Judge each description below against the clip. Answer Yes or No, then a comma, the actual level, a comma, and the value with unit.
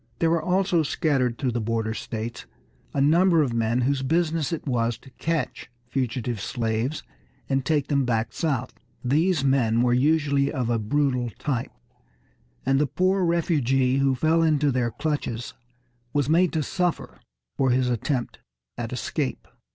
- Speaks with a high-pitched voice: No, low, 135 Hz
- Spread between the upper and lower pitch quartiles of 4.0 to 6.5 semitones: Yes, average, 4.4 semitones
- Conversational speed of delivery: Yes, average, 155 wpm